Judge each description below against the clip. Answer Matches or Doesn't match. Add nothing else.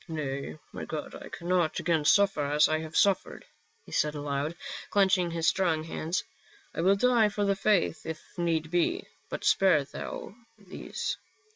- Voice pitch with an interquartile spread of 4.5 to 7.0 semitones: Doesn't match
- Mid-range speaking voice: Matches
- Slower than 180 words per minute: Matches